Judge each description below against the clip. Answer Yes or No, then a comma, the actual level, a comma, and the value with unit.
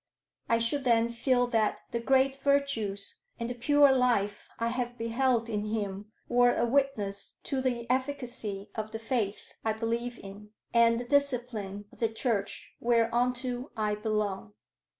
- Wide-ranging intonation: No, average, 2.8 semitones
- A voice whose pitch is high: Yes, high, 235 Hz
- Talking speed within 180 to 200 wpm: No, average, 150 wpm